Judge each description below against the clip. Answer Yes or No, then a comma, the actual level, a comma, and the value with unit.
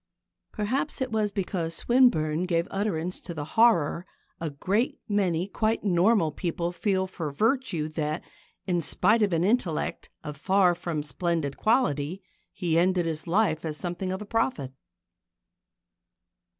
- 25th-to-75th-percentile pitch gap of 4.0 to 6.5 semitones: Yes, average, 4.6 semitones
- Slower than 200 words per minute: Yes, average, 140 wpm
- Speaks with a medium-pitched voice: Yes, medium, 180 Hz